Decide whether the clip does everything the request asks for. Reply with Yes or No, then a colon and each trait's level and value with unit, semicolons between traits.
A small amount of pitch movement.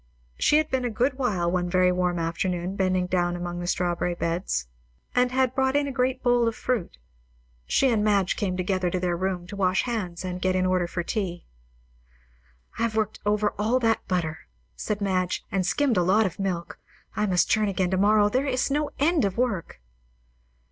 No: average, 4.7 semitones